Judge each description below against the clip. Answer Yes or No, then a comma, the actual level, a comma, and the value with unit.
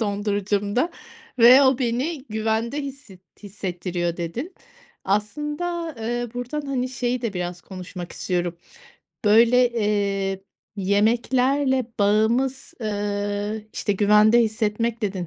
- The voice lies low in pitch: No, high, 220 Hz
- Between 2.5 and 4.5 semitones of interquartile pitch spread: Yes, average, 3.7 semitones